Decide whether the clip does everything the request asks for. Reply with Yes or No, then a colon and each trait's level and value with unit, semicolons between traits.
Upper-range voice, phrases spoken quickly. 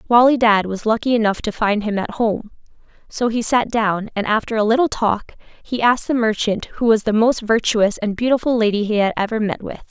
Yes: high, 220 Hz; fast, 220 wpm